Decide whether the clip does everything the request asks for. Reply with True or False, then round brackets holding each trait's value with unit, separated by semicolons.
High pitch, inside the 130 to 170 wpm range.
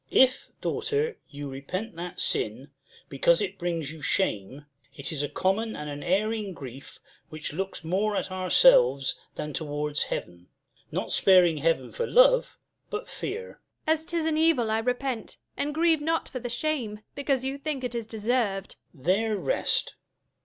True (210 Hz; 165 wpm)